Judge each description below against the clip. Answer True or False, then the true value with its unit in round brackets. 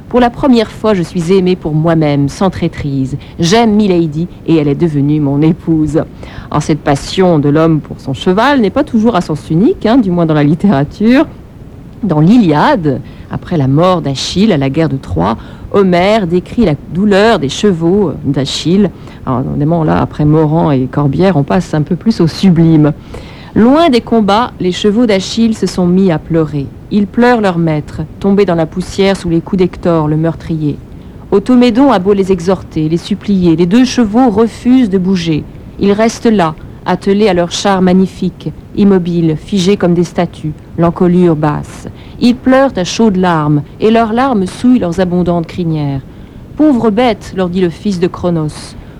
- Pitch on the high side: False (180 Hz)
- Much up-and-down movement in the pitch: False (4.7 semitones)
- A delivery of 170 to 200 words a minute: True (175 wpm)